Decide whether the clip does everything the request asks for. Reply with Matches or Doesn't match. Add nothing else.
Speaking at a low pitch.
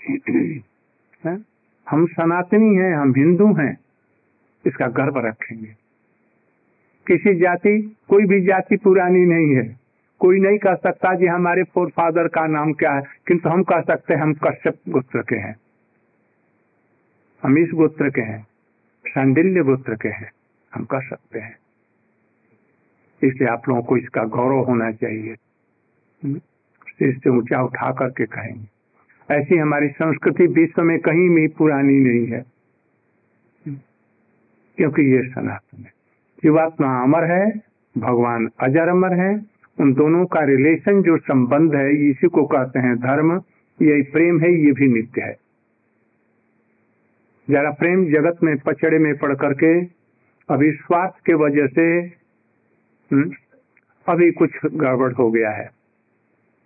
Doesn't match